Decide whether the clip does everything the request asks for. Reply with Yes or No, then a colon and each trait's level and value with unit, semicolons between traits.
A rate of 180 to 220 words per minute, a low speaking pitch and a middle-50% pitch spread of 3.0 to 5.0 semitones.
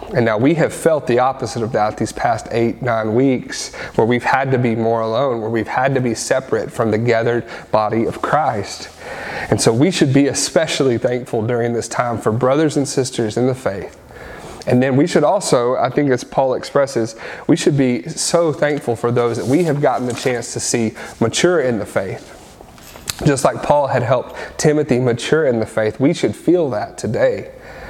Yes: average, 200 wpm; low, 120 Hz; average, 3.3 semitones